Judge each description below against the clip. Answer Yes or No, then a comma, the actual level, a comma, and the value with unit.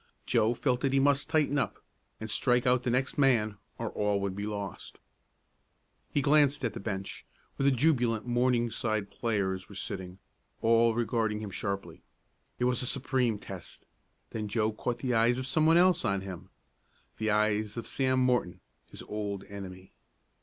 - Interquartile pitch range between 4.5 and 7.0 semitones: No, average, 3.9 semitones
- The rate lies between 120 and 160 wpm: No, average, 170 wpm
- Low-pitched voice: Yes, low, 115 Hz